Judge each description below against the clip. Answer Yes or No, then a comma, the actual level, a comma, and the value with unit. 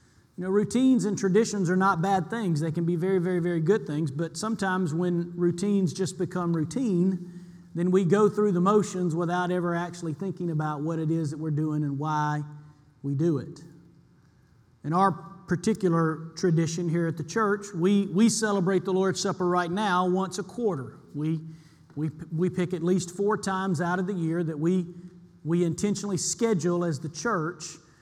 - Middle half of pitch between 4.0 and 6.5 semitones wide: No, average, 2.9 semitones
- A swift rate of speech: No, average, 180 wpm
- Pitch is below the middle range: No, medium, 175 Hz